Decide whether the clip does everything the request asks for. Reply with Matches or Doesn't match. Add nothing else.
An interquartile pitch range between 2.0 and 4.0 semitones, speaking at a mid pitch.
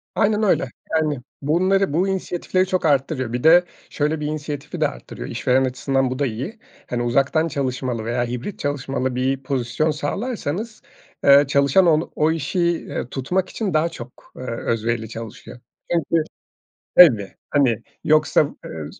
Doesn't match